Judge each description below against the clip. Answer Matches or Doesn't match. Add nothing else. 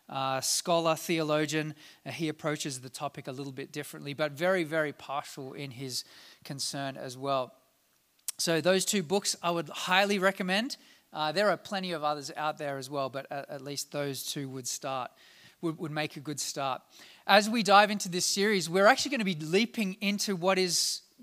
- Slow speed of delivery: Doesn't match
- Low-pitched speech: Doesn't match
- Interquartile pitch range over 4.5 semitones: Matches